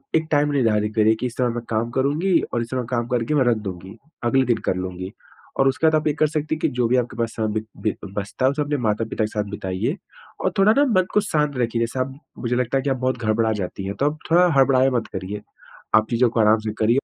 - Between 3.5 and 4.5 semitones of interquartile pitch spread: Yes, average, 3.9 semitones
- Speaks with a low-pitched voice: Yes, low, 120 Hz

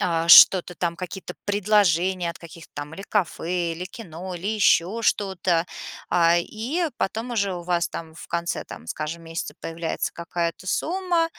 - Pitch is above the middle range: No, medium, 175 Hz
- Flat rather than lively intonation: No, average, 3.3 semitones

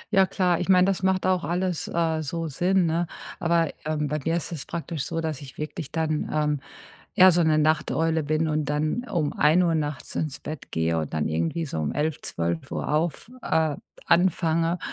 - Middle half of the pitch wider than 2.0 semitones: Yes, narrow, 2.4 semitones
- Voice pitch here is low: No, medium, 160 Hz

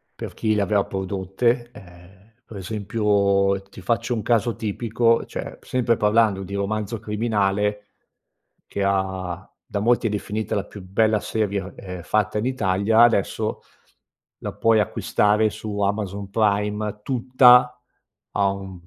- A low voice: Yes, low, 105 Hz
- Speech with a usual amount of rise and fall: No, narrow, 2.2 semitones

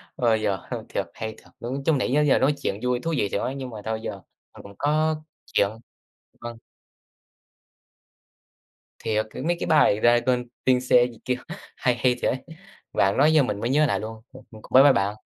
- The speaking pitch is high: No, low, 125 Hz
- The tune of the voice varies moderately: Yes, average, 3.9 semitones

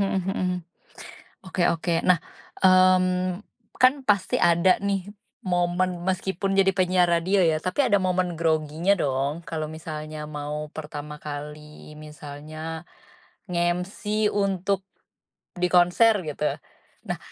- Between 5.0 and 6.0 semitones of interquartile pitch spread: No, average, 3.2 semitones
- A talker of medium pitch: Yes, medium, 175 Hz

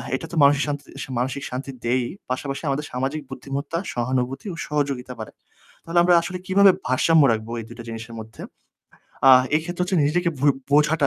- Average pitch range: Yes, average, 4.1 semitones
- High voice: No, medium, 140 Hz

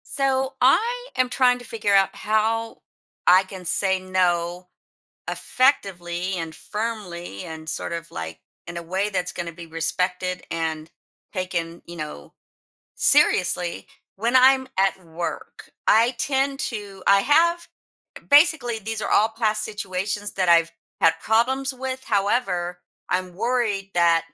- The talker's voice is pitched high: Yes, high, 195 Hz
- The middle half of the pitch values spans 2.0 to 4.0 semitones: No, wide, 5.5 semitones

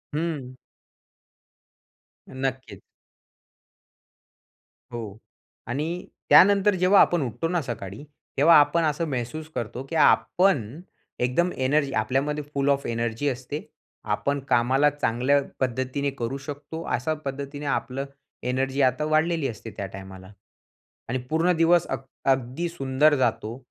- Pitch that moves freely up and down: No, average, 3.8 semitones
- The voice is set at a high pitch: No, low, 135 Hz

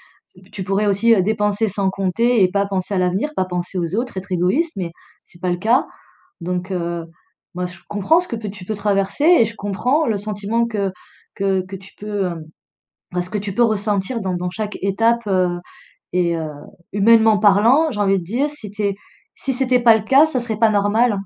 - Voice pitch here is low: No, high, 205 Hz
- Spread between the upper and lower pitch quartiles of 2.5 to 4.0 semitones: Yes, average, 3.4 semitones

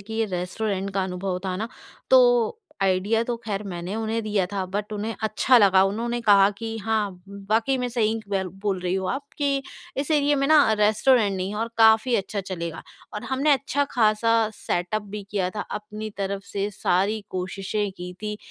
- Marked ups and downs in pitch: No, average, 2.8 semitones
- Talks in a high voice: Yes, high, 210 Hz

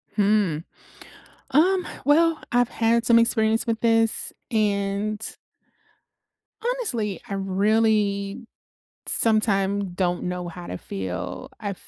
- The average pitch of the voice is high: Yes, high, 215 Hz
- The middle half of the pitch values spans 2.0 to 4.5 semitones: Yes, average, 2.8 semitones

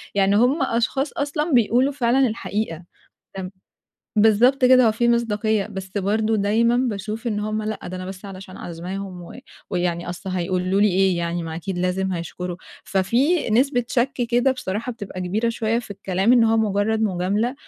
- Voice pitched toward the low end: No, high, 210 Hz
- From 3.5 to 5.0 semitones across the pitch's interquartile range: Yes, average, 4.1 semitones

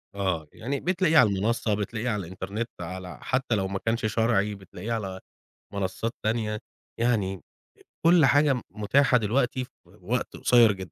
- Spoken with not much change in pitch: No, average, 4.1 semitones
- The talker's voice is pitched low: Yes, low, 110 Hz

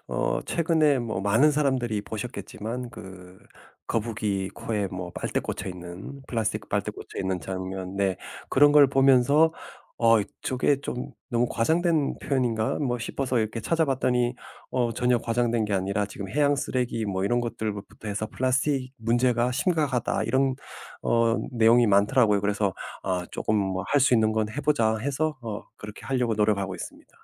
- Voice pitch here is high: No, low, 115 Hz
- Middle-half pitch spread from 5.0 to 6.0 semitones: No, average, 4.2 semitones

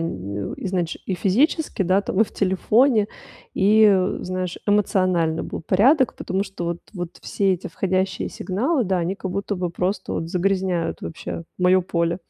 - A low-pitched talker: No, medium, 185 Hz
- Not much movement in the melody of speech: Yes, narrow, 2.2 semitones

